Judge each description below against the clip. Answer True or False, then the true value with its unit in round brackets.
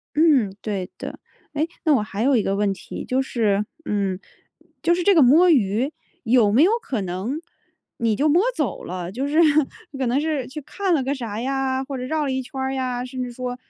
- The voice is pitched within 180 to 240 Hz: False (255 Hz)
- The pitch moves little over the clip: False (5.2 semitones)